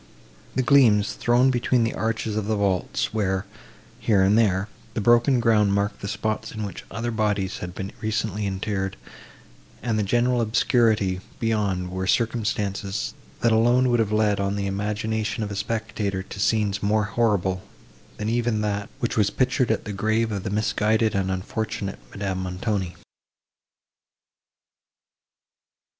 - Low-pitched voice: Yes, low, 105 Hz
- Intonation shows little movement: Yes, narrow, 2.3 semitones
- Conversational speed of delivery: Yes, average, 150 wpm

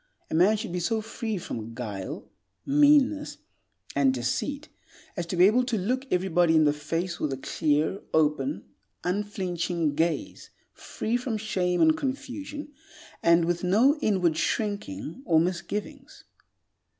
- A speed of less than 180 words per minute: Yes, average, 140 wpm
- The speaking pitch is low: No, medium, 180 Hz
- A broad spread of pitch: Yes, wide, 6.8 semitones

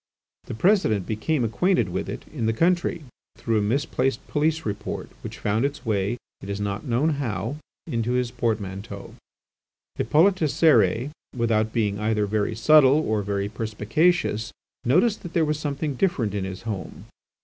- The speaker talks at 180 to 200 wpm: No, average, 155 wpm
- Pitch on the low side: Yes, low, 115 Hz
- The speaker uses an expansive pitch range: Yes, wide, 6.3 semitones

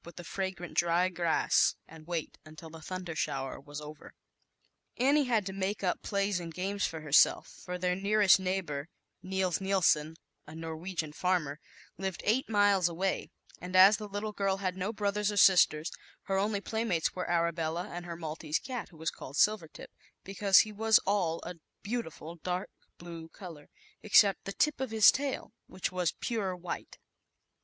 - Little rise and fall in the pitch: No, average, 3.5 semitones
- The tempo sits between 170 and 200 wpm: Yes, average, 175 wpm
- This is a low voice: No, medium, 185 Hz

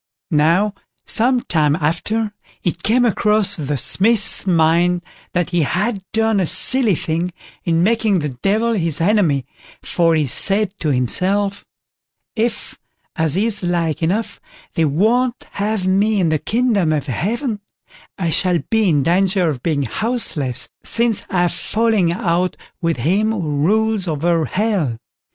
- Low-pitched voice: No, medium, 185 Hz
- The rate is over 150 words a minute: No, average, 140 wpm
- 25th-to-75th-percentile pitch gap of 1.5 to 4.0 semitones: No, average, 5.0 semitones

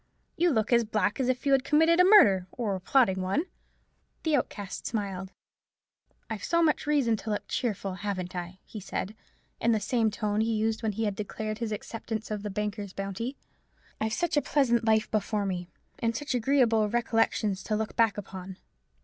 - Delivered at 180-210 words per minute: Yes, average, 190 wpm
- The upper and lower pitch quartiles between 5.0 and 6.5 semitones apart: No, average, 3.1 semitones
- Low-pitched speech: No, high, 220 Hz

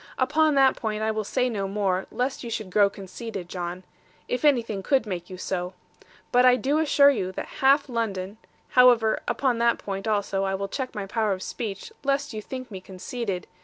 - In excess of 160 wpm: Yes, average, 200 wpm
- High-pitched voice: Yes, high, 220 Hz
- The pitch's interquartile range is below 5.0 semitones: Yes, average, 4.6 semitones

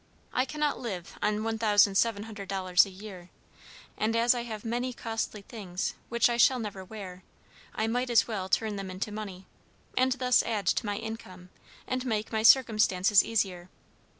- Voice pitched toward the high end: Yes, high, 215 Hz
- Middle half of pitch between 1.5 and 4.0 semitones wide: Yes, average, 3.2 semitones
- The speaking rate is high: No, average, 160 wpm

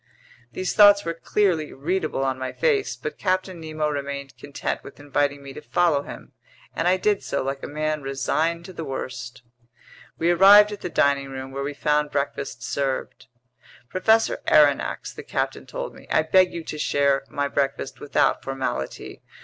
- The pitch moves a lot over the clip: No, average, 4.2 semitones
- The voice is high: No, medium, 150 Hz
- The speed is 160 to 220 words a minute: Yes, average, 175 wpm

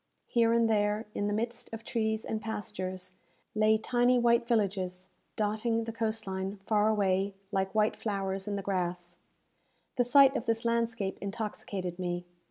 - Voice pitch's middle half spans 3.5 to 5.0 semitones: No, average, 3.0 semitones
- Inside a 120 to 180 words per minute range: Yes, average, 160 wpm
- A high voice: Yes, high, 215 Hz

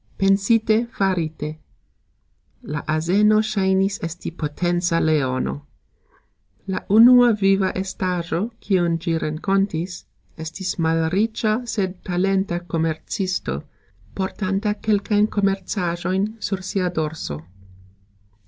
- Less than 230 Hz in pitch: Yes, medium, 185 Hz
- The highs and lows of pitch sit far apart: No, average, 3.4 semitones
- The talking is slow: Yes, slow, 85 wpm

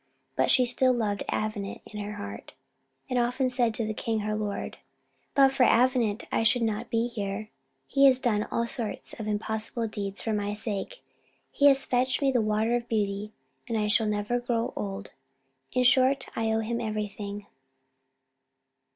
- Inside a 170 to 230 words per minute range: Yes, average, 175 wpm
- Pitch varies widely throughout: No, average, 2.7 semitones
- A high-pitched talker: Yes, high, 225 Hz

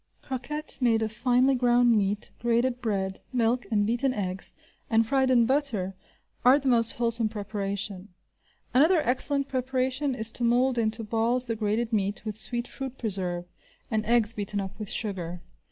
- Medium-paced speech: Yes, average, 160 wpm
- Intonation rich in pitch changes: No, average, 3.2 semitones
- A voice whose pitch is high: Yes, high, 230 Hz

